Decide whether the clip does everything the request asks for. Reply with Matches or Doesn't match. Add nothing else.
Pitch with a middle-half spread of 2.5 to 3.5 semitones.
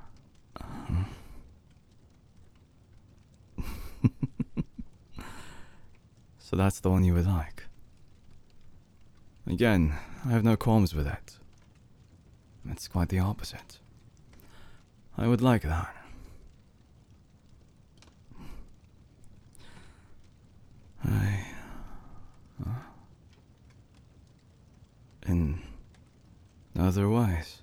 Doesn't match